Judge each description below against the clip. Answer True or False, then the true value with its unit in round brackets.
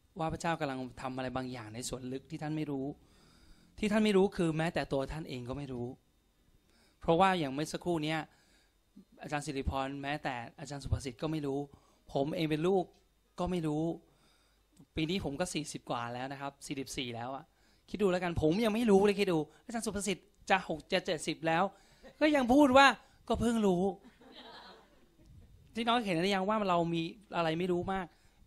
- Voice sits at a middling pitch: True (160 Hz)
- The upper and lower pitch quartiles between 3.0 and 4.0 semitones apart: False (5.6 semitones)